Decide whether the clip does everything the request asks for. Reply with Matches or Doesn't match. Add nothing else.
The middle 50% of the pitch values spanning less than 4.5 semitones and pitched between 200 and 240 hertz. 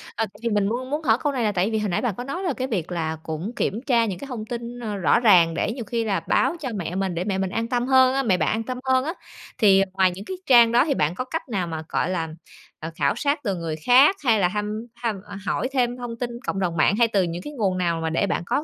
Doesn't match